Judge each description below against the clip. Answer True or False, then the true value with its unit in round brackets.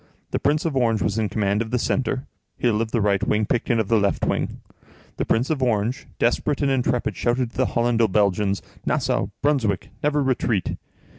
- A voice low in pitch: True (115 Hz)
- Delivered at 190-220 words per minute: True (195 wpm)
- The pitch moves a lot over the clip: False (3.7 semitones)